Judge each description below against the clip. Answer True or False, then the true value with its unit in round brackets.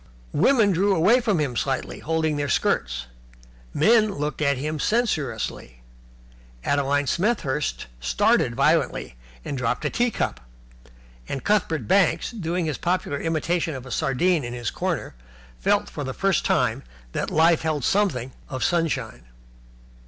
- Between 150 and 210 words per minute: False (140 wpm)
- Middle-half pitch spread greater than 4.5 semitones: True (5.6 semitones)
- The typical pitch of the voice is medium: True (155 Hz)